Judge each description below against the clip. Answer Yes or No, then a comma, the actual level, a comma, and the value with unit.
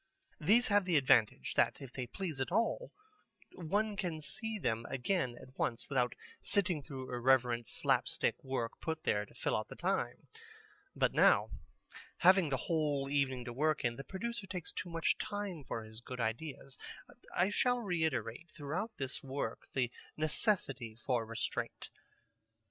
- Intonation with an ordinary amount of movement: No, wide, 6.5 semitones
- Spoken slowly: No, average, 155 wpm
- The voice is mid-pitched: Yes, medium, 145 Hz